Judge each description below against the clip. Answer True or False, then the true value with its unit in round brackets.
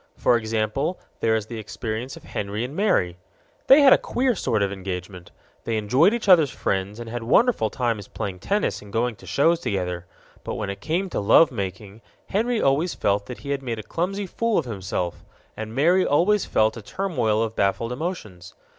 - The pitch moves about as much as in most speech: False (8.6 semitones)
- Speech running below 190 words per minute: False (195 wpm)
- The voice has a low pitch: True (115 Hz)